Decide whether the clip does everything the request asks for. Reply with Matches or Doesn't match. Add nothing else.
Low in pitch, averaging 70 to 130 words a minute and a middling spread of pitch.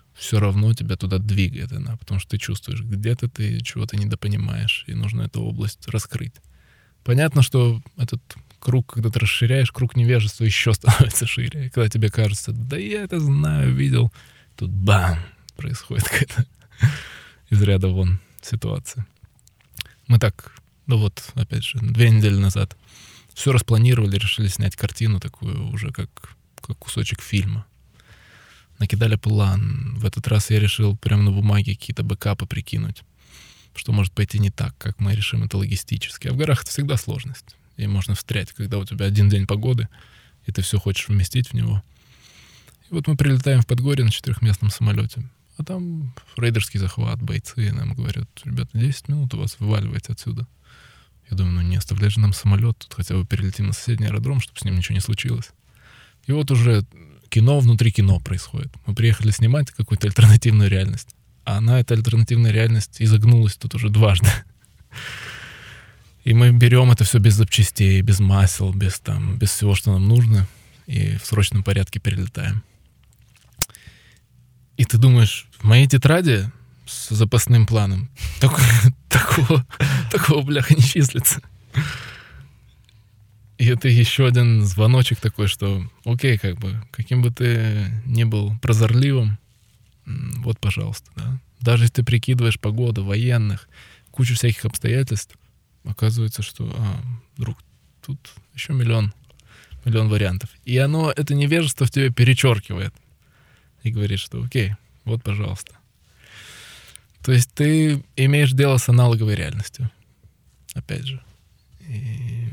Doesn't match